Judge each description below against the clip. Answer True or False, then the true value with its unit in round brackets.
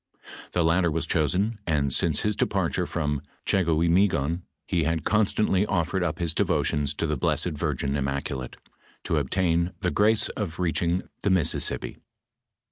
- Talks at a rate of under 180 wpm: True (145 wpm)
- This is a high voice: False (85 Hz)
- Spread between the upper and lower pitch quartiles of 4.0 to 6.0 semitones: False (3.6 semitones)